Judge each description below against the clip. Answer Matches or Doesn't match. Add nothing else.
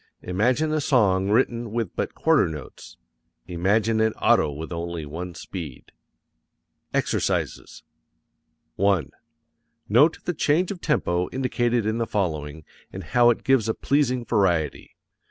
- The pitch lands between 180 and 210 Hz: Doesn't match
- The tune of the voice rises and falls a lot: Matches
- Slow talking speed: Matches